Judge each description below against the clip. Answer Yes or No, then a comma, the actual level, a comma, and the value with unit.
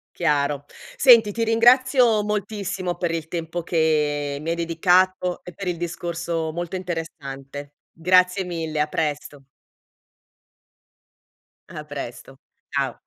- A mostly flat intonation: No, average, 3.5 semitones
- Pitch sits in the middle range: Yes, medium, 170 Hz